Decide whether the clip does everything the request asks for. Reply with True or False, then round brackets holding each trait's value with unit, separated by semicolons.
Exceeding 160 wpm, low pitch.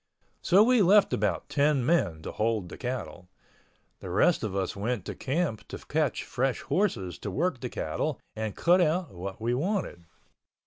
True (175 wpm; 125 Hz)